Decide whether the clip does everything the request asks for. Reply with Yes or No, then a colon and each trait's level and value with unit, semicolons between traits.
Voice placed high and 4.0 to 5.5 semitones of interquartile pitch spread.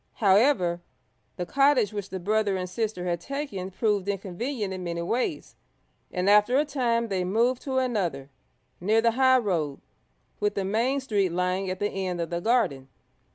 Yes: high, 205 Hz; average, 4.6 semitones